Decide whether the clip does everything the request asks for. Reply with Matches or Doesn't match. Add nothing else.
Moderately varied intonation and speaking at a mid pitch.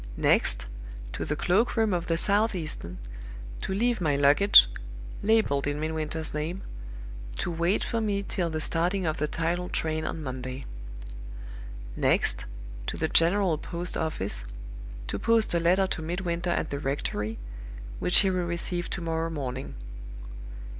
Matches